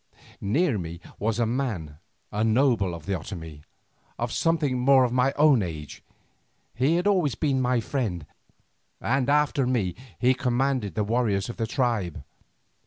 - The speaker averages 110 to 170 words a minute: Yes, average, 155 wpm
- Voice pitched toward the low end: Yes, low, 120 Hz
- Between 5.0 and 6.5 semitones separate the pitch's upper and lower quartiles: Yes, average, 5.3 semitones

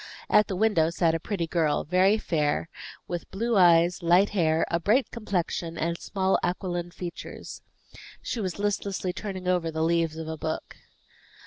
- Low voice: No, medium, 175 Hz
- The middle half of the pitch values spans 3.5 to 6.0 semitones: No, average, 2.9 semitones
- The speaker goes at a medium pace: Yes, average, 160 wpm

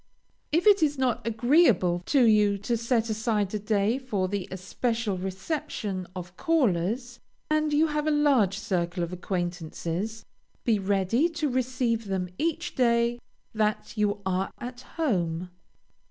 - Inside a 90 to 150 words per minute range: Yes, average, 140 wpm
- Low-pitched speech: No, high, 220 Hz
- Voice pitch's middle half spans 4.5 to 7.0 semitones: Yes, average, 5.3 semitones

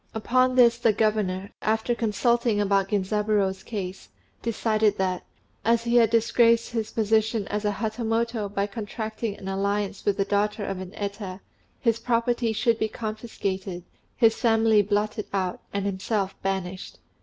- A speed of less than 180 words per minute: Yes, average, 145 wpm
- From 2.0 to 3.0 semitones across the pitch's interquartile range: Yes, narrow, 2.4 semitones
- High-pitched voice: Yes, high, 215 Hz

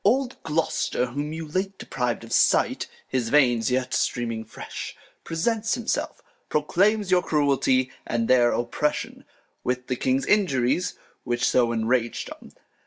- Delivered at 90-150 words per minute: Yes, slow, 135 wpm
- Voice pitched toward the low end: Yes, low, 130 Hz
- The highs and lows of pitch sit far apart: Yes, wide, 5.7 semitones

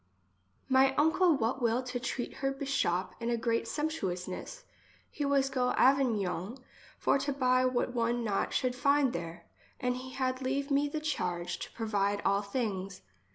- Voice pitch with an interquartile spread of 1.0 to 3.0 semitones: No, average, 4.8 semitones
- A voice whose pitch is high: Yes, very high, 250 Hz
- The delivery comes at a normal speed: Yes, average, 160 wpm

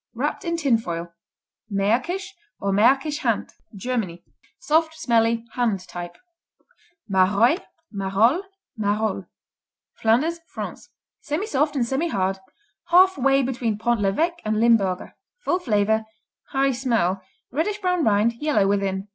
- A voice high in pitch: Yes, high, 230 Hz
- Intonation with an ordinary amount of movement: No, wide, 6.9 semitones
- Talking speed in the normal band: No, slow, 115 wpm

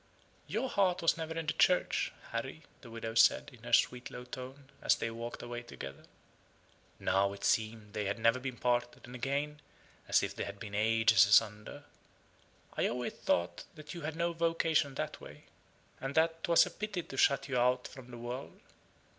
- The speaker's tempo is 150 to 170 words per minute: No, average, 185 wpm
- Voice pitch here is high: No, low, 125 Hz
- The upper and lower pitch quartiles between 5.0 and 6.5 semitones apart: Yes, wide, 5.6 semitones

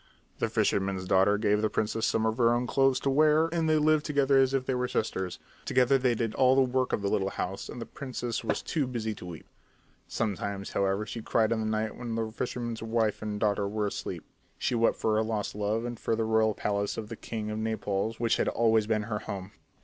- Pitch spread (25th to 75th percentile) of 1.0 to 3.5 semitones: Yes, average, 3.0 semitones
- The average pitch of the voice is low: Yes, low, 110 Hz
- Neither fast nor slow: No, fast, 235 wpm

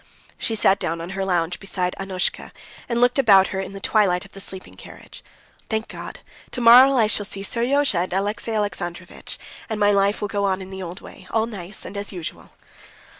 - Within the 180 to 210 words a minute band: Yes, average, 200 wpm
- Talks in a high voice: Yes, high, 195 Hz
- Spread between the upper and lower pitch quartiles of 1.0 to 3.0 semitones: Yes, average, 2.7 semitones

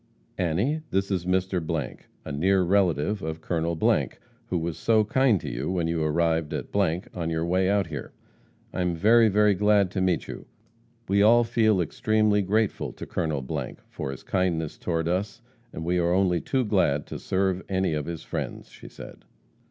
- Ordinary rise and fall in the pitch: Yes, average, 3.7 semitones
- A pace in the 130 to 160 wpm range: No, average, 175 wpm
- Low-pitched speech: Yes, very low, 90 Hz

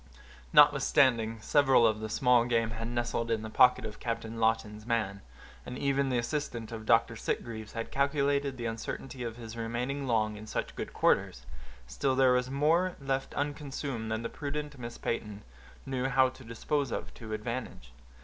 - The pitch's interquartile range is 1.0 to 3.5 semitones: Yes, average, 3.1 semitones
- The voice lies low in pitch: Yes, low, 120 Hz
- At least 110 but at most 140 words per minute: No, average, 170 wpm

